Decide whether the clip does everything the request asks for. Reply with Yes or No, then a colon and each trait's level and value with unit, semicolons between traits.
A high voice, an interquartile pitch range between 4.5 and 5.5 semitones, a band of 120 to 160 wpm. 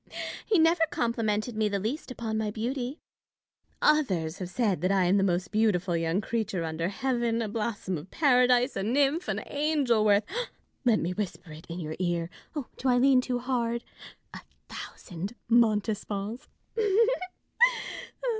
Yes: high, 220 Hz; average, 4.9 semitones; average, 155 wpm